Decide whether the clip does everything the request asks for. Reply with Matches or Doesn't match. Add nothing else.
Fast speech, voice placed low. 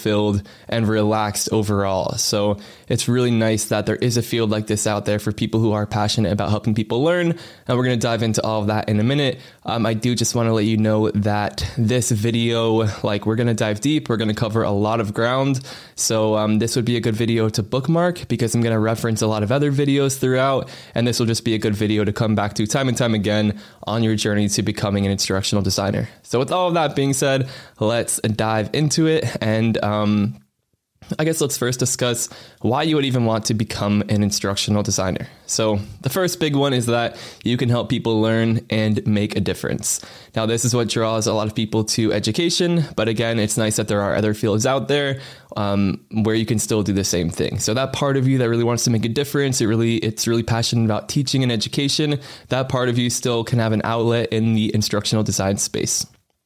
Matches